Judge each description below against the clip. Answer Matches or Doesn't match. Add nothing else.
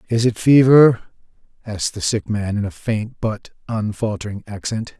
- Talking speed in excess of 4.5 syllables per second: Matches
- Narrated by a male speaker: Matches